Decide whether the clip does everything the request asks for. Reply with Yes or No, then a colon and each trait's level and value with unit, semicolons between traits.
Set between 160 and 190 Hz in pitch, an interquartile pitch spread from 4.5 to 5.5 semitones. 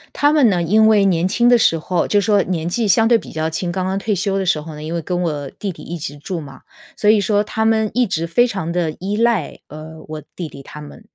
Yes: medium, 185 Hz; average, 5.1 semitones